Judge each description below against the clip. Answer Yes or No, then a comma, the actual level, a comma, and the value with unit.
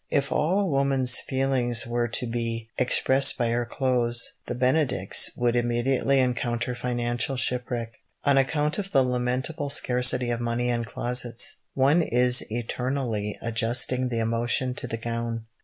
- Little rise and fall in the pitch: Yes, narrow, 1.9 semitones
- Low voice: Yes, low, 125 Hz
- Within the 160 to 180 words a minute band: No, average, 145 wpm